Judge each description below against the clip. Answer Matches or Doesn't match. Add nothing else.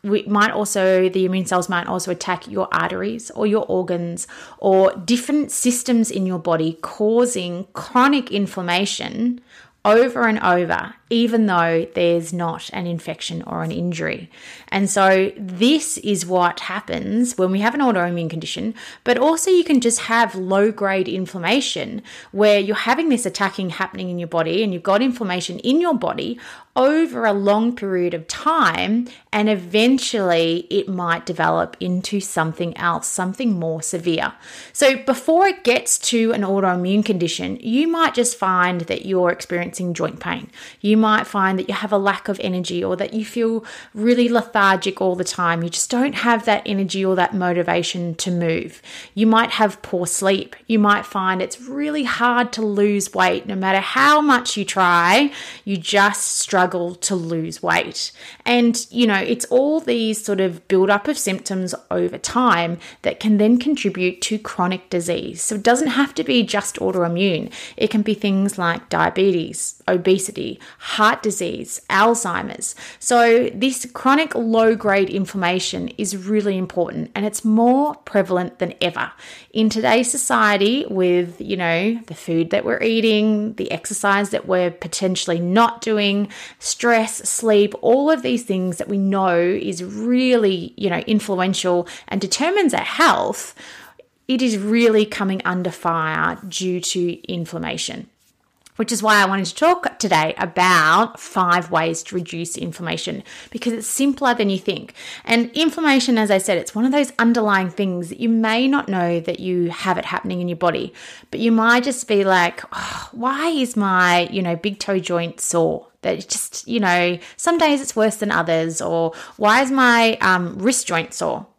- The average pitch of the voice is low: Doesn't match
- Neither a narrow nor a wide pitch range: Matches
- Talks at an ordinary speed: Matches